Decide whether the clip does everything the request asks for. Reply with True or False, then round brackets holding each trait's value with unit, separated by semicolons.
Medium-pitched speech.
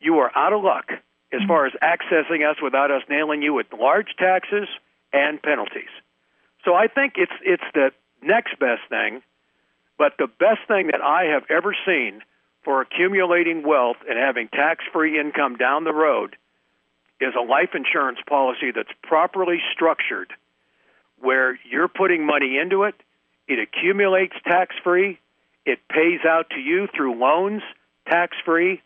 True (160 Hz)